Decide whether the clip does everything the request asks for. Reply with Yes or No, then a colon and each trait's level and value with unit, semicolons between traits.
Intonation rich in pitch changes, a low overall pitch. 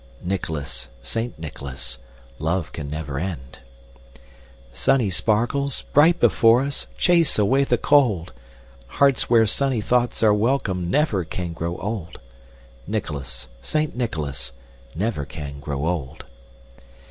Yes: wide, 8.5 semitones; very low, 95 Hz